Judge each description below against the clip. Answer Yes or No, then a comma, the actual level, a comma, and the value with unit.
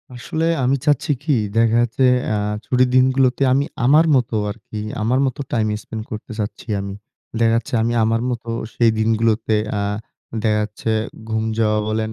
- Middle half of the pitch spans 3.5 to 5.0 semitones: No, average, 2.7 semitones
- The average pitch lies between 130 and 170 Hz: No, low, 115 Hz